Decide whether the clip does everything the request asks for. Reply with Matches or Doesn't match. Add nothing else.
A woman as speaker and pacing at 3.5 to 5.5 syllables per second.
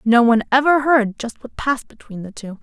Doesn't match